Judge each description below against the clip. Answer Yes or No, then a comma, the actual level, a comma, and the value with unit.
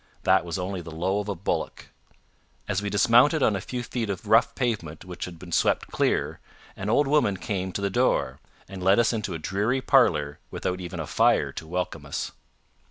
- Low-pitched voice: Yes, low, 100 Hz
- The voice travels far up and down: No, average, 4.2 semitones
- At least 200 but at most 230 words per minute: Yes, fast, 205 wpm